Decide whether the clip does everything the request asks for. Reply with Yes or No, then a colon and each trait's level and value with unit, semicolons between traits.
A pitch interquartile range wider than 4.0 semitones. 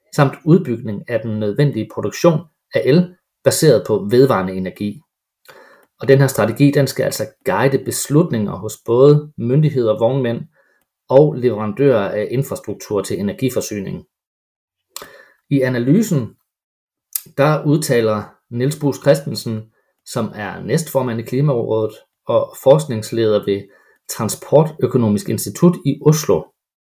Yes: average, 4.7 semitones